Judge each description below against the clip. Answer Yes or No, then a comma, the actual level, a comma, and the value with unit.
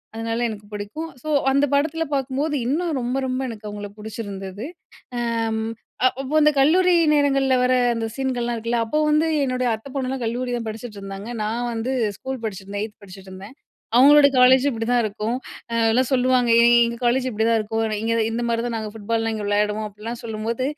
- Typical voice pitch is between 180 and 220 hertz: No, high, 235 Hz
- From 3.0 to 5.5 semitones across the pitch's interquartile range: Yes, average, 3.3 semitones